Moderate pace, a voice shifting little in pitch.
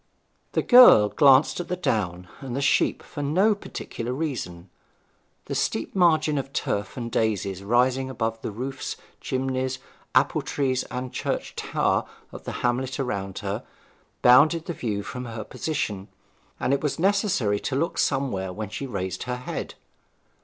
No: average, 155 wpm; average, 4.9 semitones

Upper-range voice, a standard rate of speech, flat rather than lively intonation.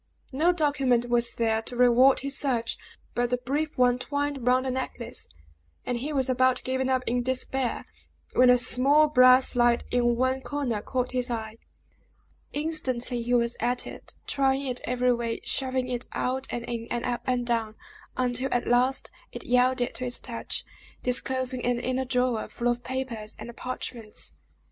Yes: very high, 250 Hz; average, 170 wpm; narrow, 1.5 semitones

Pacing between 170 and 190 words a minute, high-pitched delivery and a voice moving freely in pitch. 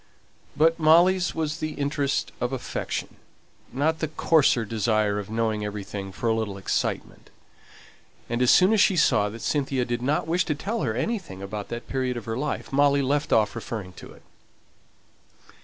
No: average, 175 wpm; low, 125 Hz; wide, 6.1 semitones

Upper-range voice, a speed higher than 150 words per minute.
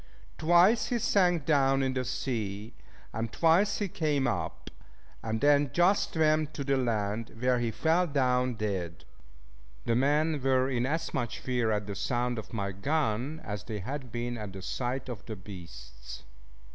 No: low, 125 Hz; average, 170 wpm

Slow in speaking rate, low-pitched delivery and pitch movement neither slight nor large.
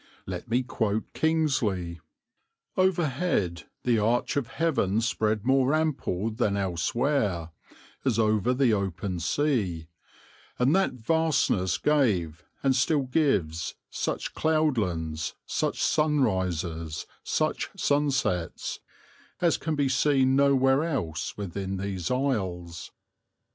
No: slow, 105 wpm; low, 115 Hz; wide, 7.5 semitones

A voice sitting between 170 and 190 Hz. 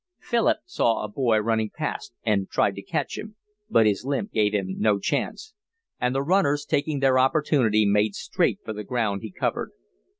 No: low, 115 Hz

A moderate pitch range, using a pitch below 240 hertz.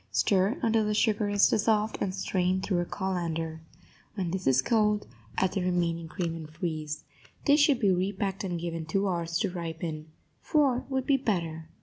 Yes: average, 4.0 semitones; medium, 185 Hz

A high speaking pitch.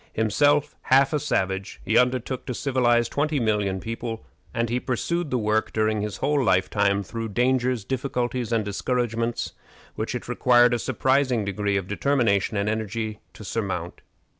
No: low, 115 Hz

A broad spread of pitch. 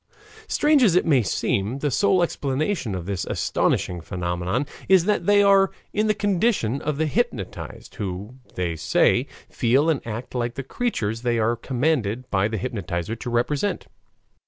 Yes: wide, 8.4 semitones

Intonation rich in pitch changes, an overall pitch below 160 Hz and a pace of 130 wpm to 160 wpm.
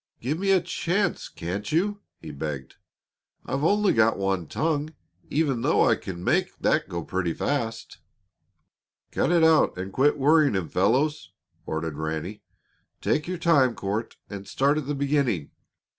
Yes: wide, 8.6 semitones; low, 135 Hz; average, 155 wpm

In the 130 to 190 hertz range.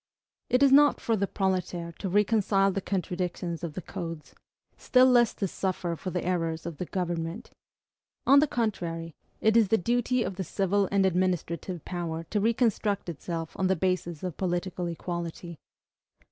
Yes: medium, 185 Hz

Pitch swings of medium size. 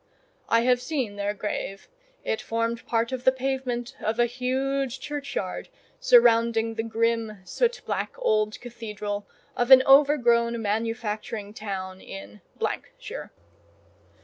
Yes: average, 3.4 semitones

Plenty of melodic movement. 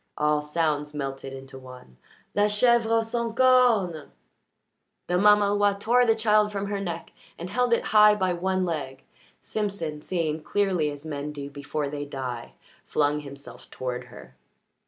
Yes: wide, 6.4 semitones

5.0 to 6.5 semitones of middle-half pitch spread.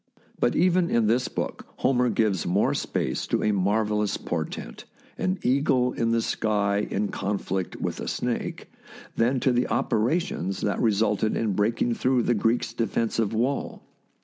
No: average, 3.2 semitones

